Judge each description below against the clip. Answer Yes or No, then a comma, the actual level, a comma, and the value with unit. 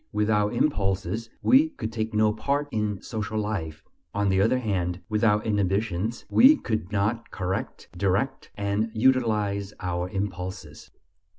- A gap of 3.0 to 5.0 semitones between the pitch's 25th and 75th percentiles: No, narrow, 2.6 semitones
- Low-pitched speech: Yes, low, 105 Hz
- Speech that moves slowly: Yes, slow, 130 wpm